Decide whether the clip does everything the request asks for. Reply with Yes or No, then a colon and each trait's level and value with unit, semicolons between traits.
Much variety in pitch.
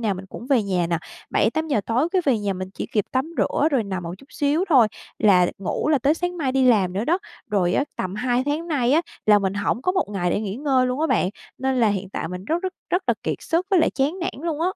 Yes: wide, 7.6 semitones